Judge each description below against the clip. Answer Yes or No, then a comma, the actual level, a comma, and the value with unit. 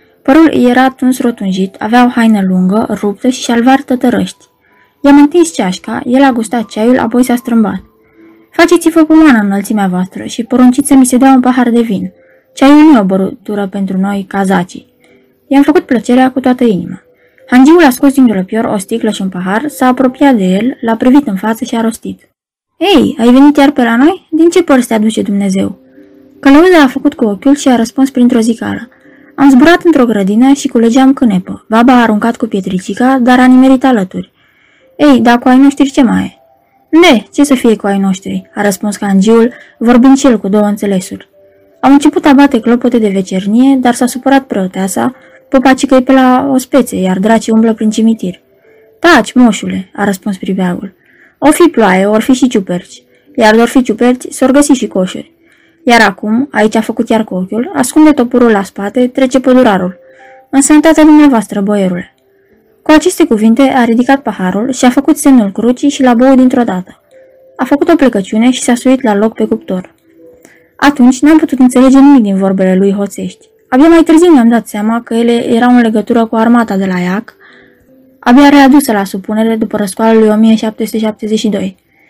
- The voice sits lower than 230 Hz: No, high, 240 Hz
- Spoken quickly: Yes, fast, 185 wpm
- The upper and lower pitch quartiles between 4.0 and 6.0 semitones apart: Yes, average, 4.5 semitones